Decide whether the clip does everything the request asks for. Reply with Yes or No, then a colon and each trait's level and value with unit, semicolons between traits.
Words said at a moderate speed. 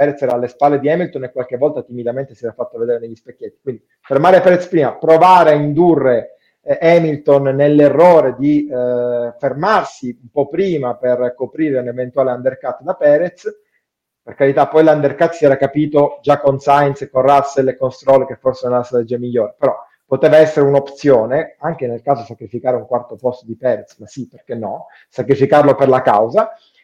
No: fast, 185 wpm